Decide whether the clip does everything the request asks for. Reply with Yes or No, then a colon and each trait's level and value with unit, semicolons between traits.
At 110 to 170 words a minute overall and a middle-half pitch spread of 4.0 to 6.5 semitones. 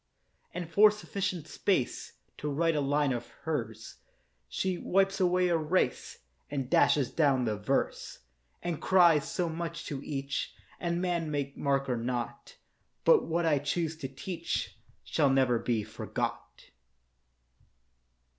Yes: slow, 135 wpm; average, 4.4 semitones